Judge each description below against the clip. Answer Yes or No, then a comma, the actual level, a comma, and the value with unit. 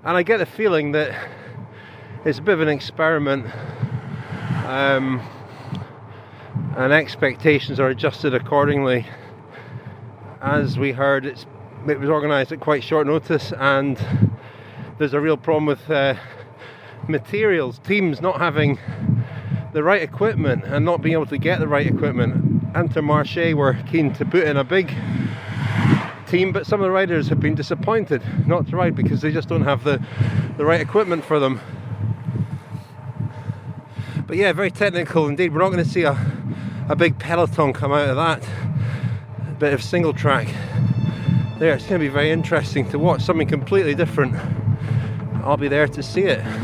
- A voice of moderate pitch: Yes, medium, 145 Hz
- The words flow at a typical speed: Yes, average, 160 wpm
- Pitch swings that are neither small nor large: Yes, average, 3.5 semitones